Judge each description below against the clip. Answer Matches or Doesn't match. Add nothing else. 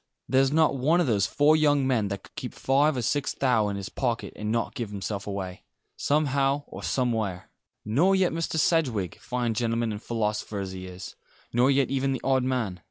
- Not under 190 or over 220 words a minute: Matches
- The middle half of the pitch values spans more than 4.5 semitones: Matches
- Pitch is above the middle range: Doesn't match